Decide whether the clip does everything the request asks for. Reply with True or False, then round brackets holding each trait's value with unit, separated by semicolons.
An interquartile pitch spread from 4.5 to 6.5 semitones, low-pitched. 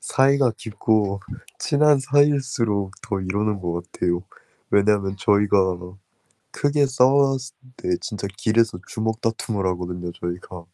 True (5.6 semitones; 105 Hz)